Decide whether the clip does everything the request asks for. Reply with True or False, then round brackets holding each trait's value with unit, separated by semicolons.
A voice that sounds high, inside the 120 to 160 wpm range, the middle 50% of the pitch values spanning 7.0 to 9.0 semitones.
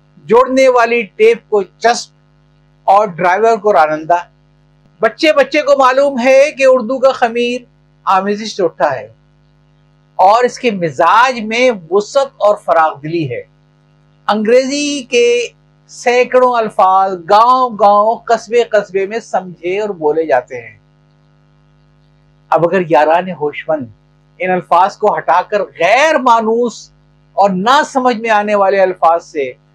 True (195 Hz; 125 wpm; 8.2 semitones)